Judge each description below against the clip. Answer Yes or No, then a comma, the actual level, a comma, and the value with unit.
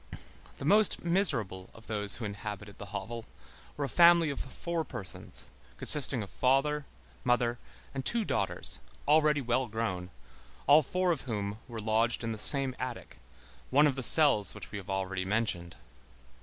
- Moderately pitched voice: No, low, 120 Hz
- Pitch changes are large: Yes, wide, 6.0 semitones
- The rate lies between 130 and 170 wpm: Yes, average, 160 wpm